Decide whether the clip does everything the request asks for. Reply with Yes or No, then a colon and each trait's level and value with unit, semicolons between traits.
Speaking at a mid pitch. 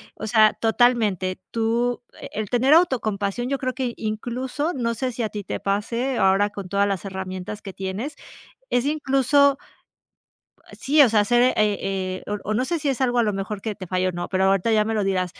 No: high, 220 Hz